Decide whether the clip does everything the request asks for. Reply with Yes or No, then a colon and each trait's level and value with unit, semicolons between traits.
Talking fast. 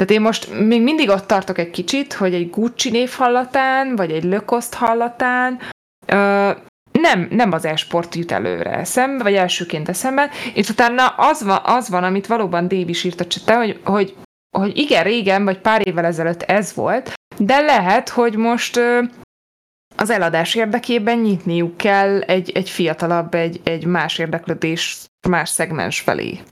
Yes: fast, 160 wpm